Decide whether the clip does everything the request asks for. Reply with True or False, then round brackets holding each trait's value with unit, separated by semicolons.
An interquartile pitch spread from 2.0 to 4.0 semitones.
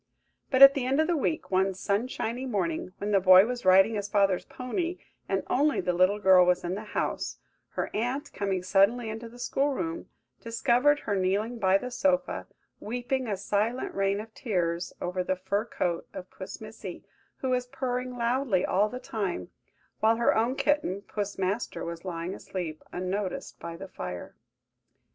False (5.0 semitones)